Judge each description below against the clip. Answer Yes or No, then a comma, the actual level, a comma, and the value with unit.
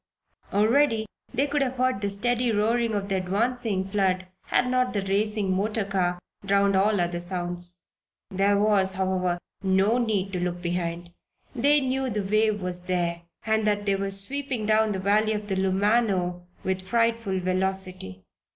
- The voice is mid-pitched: No, high, 200 Hz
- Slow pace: No, average, 160 wpm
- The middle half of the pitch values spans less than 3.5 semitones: Yes, average, 2.9 semitones